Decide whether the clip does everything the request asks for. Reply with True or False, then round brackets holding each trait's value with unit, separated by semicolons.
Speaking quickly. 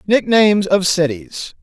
False (110 wpm)